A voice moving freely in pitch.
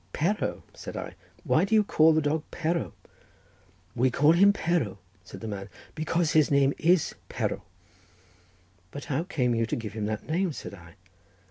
Yes: wide, 6.8 semitones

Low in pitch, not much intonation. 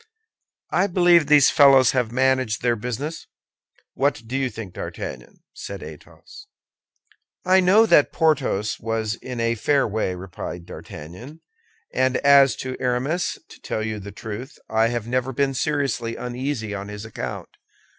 No: low, 125 Hz; average, 4.2 semitones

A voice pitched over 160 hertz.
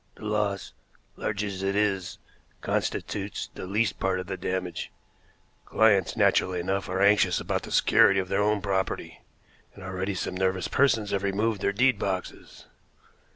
No: low, 100 Hz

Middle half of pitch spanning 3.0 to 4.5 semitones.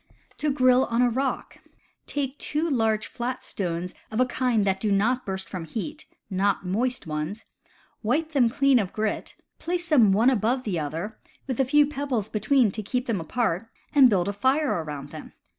No: average, 5.0 semitones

